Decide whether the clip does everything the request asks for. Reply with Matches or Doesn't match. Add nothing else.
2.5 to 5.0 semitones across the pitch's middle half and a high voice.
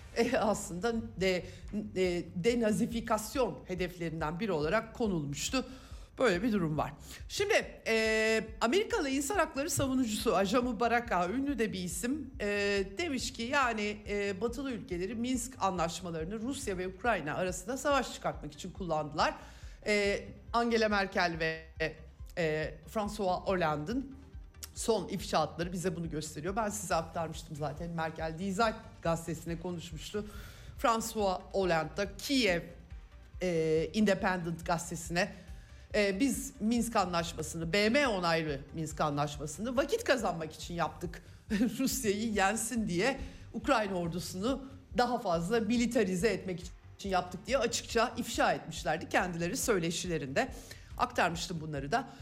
Doesn't match